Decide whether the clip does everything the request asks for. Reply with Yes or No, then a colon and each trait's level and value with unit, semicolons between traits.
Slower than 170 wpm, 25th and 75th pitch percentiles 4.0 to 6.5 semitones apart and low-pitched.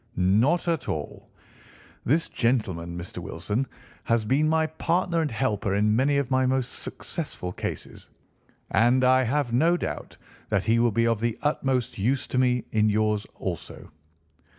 Yes: average, 155 wpm; average, 4.6 semitones; low, 125 Hz